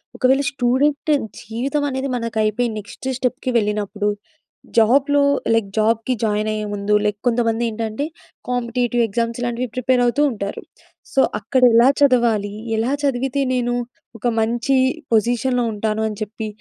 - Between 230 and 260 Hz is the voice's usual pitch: Yes, high, 235 Hz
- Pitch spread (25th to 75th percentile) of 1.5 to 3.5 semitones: Yes, average, 2.8 semitones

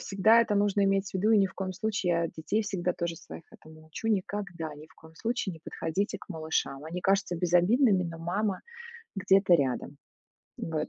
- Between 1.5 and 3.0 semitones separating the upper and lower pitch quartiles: No, average, 3.6 semitones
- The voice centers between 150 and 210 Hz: Yes, medium, 185 Hz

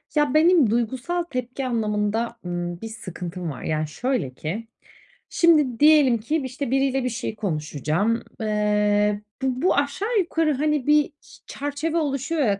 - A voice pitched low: No, high, 245 Hz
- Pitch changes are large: Yes, wide, 5.9 semitones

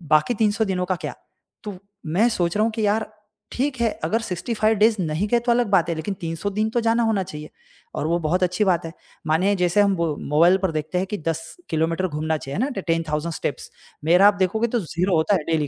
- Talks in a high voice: No, medium, 180 Hz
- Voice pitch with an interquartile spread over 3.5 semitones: Yes, average, 4.7 semitones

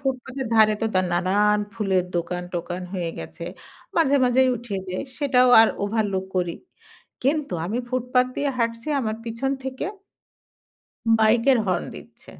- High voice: Yes, high, 225 Hz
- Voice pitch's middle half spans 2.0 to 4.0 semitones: No, average, 5.3 semitones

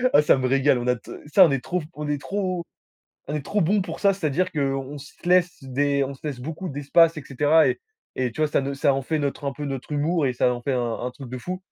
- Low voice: No, medium, 145 Hz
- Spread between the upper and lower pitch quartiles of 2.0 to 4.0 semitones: Yes, average, 3.5 semitones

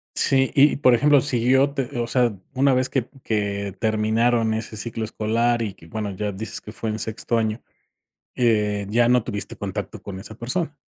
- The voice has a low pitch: Yes, low, 115 Hz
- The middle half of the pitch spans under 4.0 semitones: Yes, average, 2.8 semitones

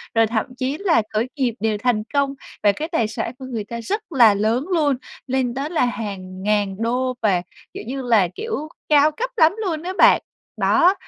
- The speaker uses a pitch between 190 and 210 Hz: No, very high, 250 Hz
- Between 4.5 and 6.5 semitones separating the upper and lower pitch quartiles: Yes, wide, 5.6 semitones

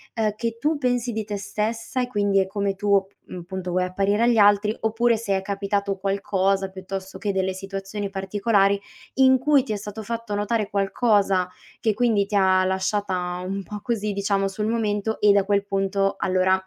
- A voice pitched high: Yes, high, 200 Hz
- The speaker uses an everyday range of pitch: No, narrow, 2.0 semitones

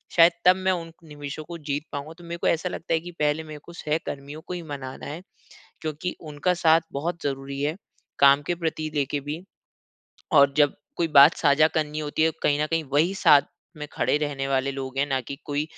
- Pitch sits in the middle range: Yes, medium, 150 Hz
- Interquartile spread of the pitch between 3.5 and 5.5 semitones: No, narrow, 2.5 semitones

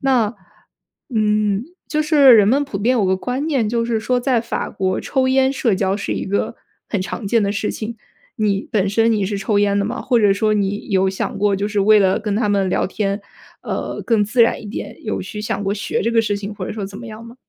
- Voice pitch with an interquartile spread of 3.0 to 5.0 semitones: No, narrow, 2.6 semitones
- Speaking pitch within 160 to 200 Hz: No, high, 210 Hz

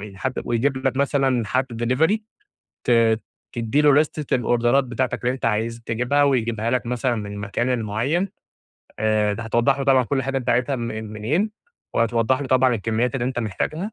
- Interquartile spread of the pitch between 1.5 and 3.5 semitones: Yes, average, 2.9 semitones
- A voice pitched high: No, low, 125 Hz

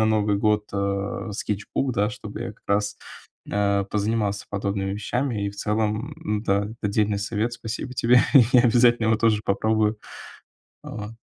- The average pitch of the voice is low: Yes, low, 105 Hz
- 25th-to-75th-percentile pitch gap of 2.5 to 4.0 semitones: No, narrow, 1.8 semitones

